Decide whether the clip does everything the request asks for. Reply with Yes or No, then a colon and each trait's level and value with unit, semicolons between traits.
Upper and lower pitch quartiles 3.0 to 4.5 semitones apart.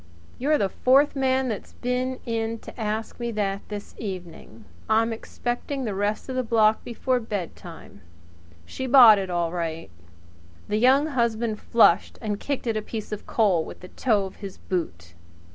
Yes: average, 4.1 semitones